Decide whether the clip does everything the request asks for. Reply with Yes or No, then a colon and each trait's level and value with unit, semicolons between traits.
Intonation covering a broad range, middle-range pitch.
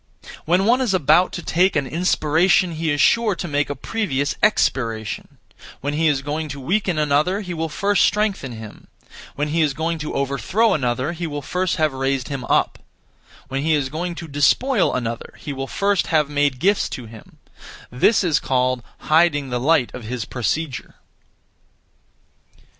No: average, 4.7 semitones; medium, 150 Hz